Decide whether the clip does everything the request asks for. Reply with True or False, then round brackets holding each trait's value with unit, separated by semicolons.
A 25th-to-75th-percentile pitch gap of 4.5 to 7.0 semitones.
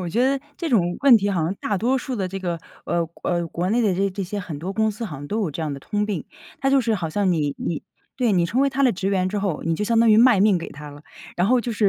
True (4.8 semitones)